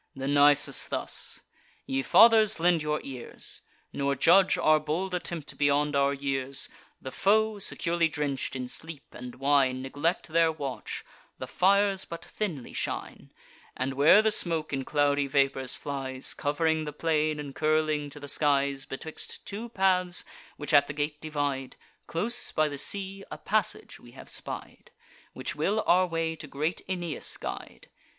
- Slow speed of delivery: No, average, 155 wpm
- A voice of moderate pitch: Yes, medium, 150 Hz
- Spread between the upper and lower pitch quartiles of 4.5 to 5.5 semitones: No, average, 3.7 semitones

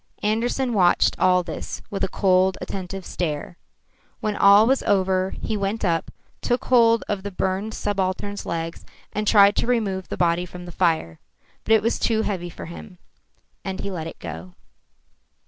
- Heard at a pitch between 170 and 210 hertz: Yes, high, 190 Hz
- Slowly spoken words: No, average, 170 wpm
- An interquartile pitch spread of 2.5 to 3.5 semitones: Yes, average, 2.9 semitones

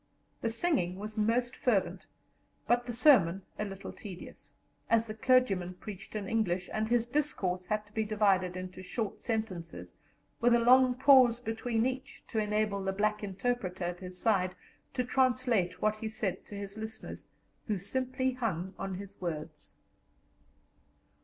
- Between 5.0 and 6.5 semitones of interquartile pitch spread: No, average, 4.3 semitones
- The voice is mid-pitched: No, high, 215 Hz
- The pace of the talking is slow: No, average, 155 wpm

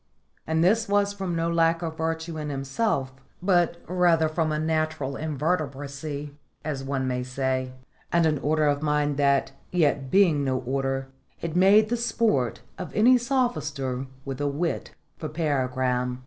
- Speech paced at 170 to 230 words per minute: No, average, 155 wpm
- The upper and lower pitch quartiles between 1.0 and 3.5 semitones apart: No, average, 4.0 semitones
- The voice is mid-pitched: Yes, medium, 155 Hz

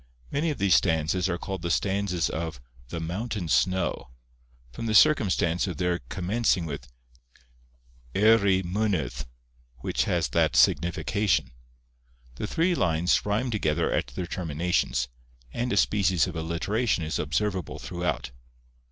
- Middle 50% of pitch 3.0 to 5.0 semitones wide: Yes, average, 4.1 semitones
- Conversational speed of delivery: No, slow, 130 wpm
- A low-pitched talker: Yes, very low, 90 Hz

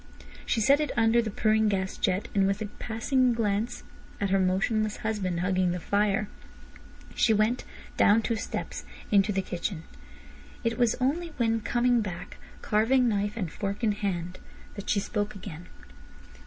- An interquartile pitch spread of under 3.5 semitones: Yes, average, 2.7 semitones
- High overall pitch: Yes, high, 210 Hz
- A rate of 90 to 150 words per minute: No, average, 160 wpm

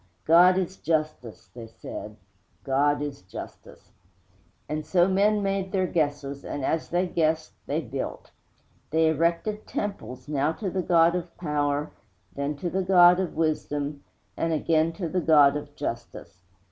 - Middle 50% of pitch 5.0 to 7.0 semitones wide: No, average, 3.6 semitones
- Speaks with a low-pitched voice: No, medium, 160 Hz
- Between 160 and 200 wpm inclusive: No, average, 150 wpm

